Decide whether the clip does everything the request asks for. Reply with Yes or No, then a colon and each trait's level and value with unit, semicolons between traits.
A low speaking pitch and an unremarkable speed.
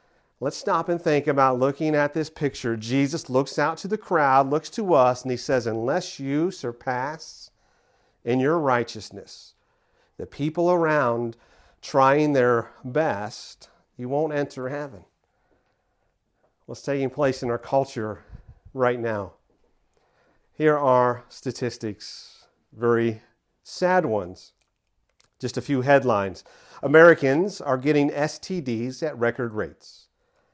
No: low, 130 Hz; slow, 125 wpm